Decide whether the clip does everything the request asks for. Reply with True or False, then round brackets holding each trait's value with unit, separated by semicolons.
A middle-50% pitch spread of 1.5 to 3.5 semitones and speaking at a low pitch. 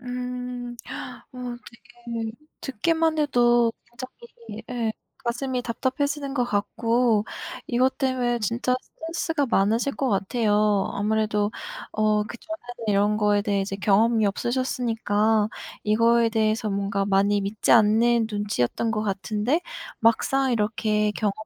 False (2.9 semitones; 230 Hz)